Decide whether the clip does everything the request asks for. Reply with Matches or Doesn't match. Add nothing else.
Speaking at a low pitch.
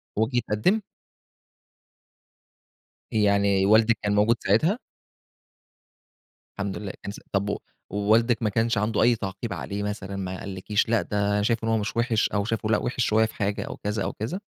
Matches